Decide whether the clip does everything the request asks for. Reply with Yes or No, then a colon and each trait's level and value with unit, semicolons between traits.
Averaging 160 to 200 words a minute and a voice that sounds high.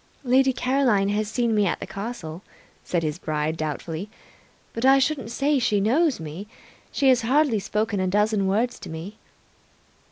Yes: average, 165 wpm; high, 215 Hz